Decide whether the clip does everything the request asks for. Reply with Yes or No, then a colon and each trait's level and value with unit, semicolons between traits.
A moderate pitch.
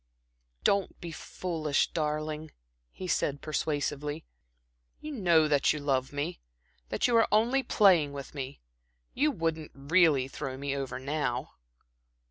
Yes: medium, 155 Hz